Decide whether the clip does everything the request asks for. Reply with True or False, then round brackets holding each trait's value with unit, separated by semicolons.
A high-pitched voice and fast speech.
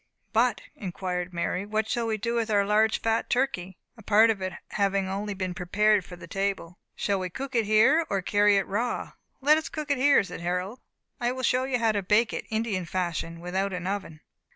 True (205 Hz; 215 wpm)